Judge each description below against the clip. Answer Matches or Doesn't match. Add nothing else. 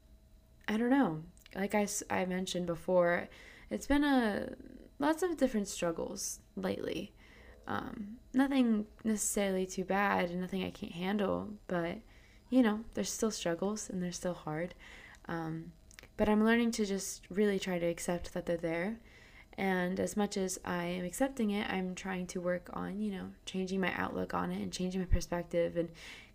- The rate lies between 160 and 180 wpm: Matches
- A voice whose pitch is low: Doesn't match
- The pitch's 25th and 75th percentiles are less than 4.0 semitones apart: Matches